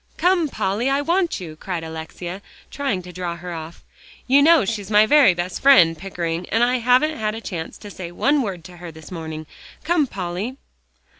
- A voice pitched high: Yes, high, 195 Hz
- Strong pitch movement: Yes, wide, 7.3 semitones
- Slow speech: No, average, 195 wpm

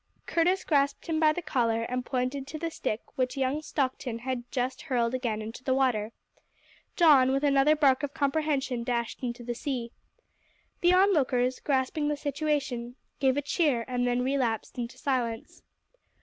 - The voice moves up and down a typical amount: Yes, average, 3.1 semitones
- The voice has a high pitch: Yes, very high, 260 Hz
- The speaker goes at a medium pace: Yes, average, 165 wpm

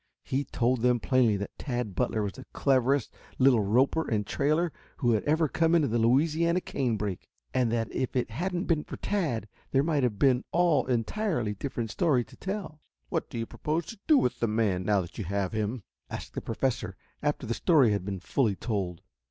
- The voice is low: Yes, low, 125 Hz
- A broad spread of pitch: Yes, wide, 5.7 semitones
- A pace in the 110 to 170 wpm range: No, average, 200 wpm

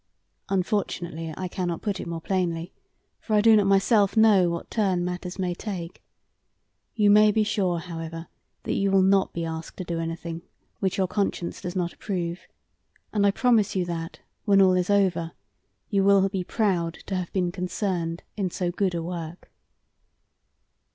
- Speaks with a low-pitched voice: No, medium, 185 Hz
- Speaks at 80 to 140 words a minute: No, average, 170 wpm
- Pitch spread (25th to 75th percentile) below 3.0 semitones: Yes, narrow, 2.6 semitones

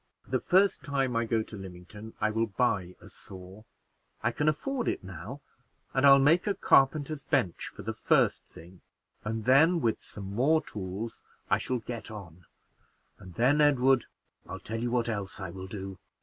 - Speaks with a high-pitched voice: No, low, 115 Hz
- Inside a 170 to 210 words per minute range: Yes, average, 180 wpm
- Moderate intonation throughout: No, wide, 6.2 semitones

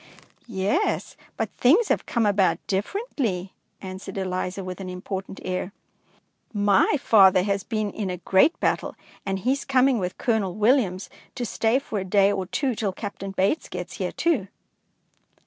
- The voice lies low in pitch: No, high, 200 Hz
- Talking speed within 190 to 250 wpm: No, average, 160 wpm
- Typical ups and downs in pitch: Yes, average, 3.9 semitones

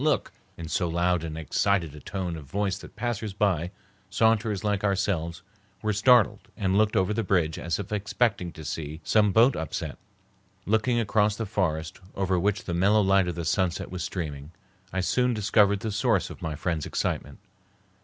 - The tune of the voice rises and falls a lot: No, average, 3.8 semitones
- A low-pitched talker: Yes, very low, 95 Hz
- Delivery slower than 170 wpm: No, average, 180 wpm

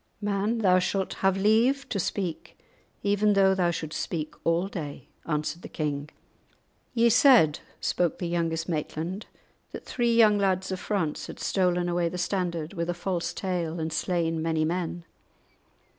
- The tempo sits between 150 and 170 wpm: Yes, average, 160 wpm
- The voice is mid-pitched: Yes, medium, 180 Hz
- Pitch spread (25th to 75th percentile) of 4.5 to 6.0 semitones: No, average, 3.2 semitones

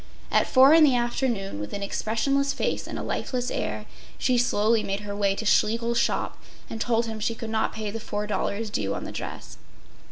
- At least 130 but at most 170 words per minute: No, average, 200 wpm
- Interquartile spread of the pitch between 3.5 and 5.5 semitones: No, average, 2.7 semitones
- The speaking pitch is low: No, high, 225 Hz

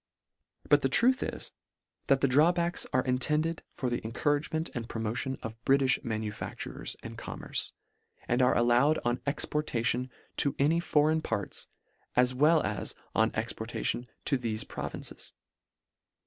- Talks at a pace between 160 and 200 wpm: No, average, 150 wpm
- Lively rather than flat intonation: No, average, 4.3 semitones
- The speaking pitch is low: Yes, low, 130 Hz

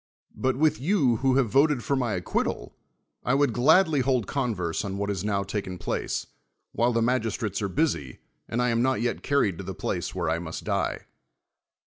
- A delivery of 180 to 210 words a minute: Yes, average, 190 wpm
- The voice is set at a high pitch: No, low, 120 Hz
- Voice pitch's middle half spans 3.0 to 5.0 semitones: No, wide, 5.4 semitones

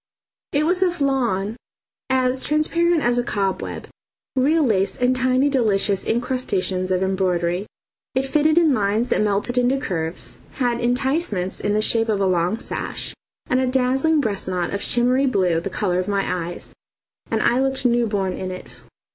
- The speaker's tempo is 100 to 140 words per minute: No, average, 170 wpm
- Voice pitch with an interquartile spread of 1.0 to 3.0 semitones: No, wide, 5.4 semitones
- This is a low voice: No, high, 235 Hz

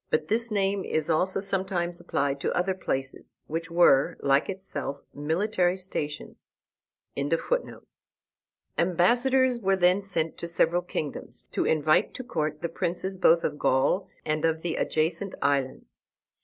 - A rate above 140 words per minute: No, slow, 135 wpm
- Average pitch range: Yes, average, 3.8 semitones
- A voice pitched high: No, medium, 175 Hz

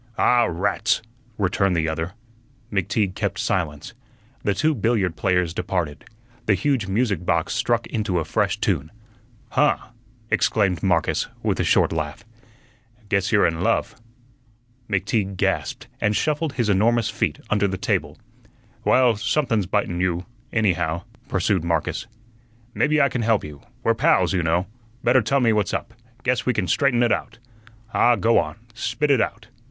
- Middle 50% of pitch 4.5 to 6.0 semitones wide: Yes, average, 4.9 semitones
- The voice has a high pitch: No, low, 100 Hz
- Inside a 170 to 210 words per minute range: No, average, 155 wpm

